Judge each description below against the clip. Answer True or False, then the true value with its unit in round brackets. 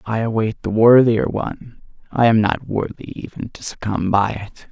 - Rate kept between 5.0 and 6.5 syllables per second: False (4.7 syllables/s)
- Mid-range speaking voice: False (110 Hz)